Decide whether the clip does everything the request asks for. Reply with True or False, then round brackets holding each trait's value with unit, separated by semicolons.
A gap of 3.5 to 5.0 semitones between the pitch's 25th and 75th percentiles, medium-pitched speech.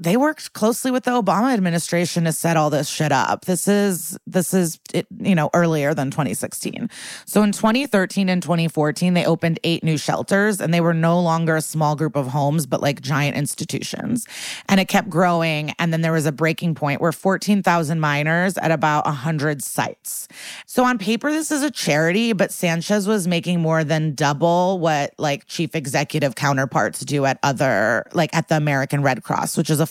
True (3.9 semitones; 165 Hz)